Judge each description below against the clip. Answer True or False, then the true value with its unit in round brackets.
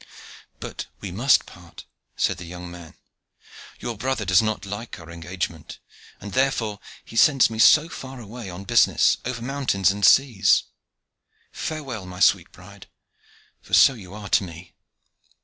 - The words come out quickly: False (150 wpm)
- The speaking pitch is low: True (105 Hz)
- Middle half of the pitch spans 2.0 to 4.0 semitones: False (5.1 semitones)